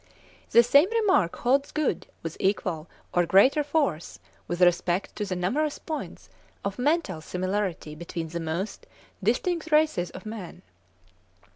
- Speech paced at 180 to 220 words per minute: No, slow, 135 wpm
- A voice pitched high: Yes, high, 200 Hz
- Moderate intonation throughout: No, wide, 8.9 semitones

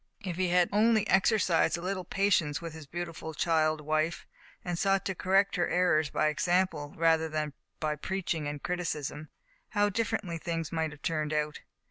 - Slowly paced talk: No, average, 170 wpm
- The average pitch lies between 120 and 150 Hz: No, medium, 170 Hz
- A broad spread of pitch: No, average, 3.2 semitones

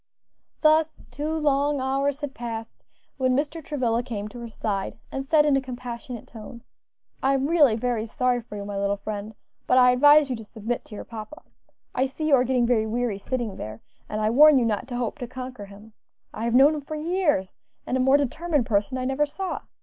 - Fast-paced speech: Yes, fast, 215 wpm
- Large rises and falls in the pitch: No, average, 4.3 semitones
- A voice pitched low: No, very high, 250 Hz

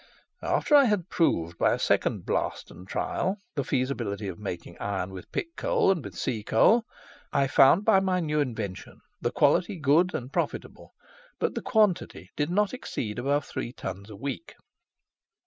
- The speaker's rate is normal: Yes, average, 165 wpm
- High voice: No, medium, 140 Hz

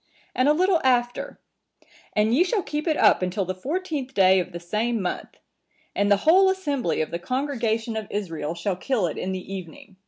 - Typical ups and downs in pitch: No, wide, 7.6 semitones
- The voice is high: Yes, high, 220 Hz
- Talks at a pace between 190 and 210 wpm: Yes, average, 195 wpm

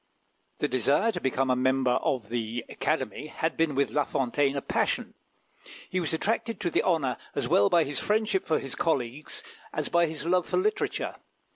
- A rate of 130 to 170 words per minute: No, average, 185 wpm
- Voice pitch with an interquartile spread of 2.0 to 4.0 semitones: No, average, 5.0 semitones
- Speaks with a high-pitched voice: No, medium, 145 Hz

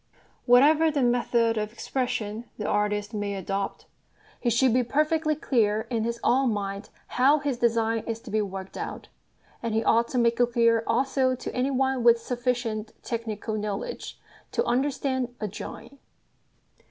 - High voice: Yes, high, 235 Hz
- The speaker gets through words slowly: No, average, 160 wpm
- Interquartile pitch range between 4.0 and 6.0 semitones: No, average, 3.0 semitones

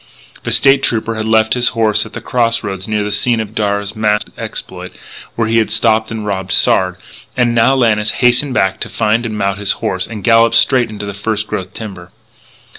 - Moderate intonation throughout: No, narrow, 2.1 semitones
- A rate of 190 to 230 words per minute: Yes, fast, 205 wpm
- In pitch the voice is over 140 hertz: No, low, 110 Hz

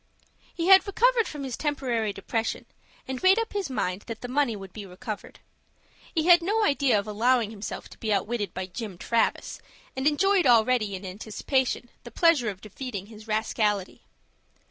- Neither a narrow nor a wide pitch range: No, wide, 5.9 semitones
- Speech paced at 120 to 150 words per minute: No, average, 170 wpm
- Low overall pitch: No, high, 235 Hz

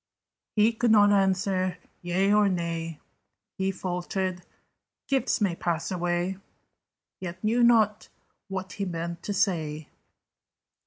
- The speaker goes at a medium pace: No, slow, 115 wpm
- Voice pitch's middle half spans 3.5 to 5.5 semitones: No, average, 2.8 semitones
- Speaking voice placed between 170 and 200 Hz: Yes, medium, 185 Hz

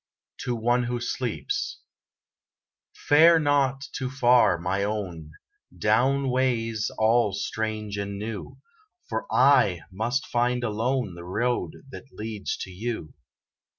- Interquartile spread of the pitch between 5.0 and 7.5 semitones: No, average, 3.8 semitones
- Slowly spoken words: Yes, slow, 120 wpm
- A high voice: No, low, 115 Hz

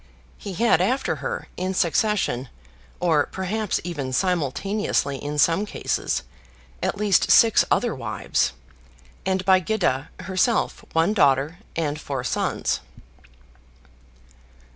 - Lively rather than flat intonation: Yes, wide, 5.9 semitones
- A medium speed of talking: No, slow, 110 wpm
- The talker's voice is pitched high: No, medium, 180 Hz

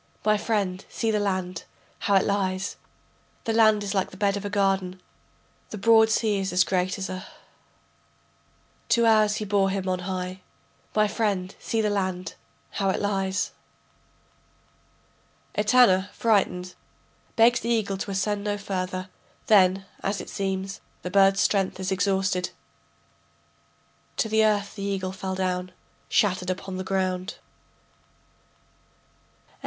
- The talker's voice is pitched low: No, high, 195 Hz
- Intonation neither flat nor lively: No, narrow, 1.9 semitones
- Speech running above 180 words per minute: No, average, 145 wpm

